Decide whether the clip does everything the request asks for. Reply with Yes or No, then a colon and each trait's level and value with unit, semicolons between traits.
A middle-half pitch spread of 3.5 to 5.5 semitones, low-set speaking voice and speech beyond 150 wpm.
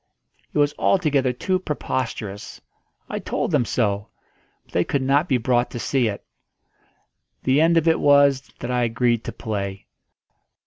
Yes: average, 4.0 semitones; low, 130 Hz; average, 160 wpm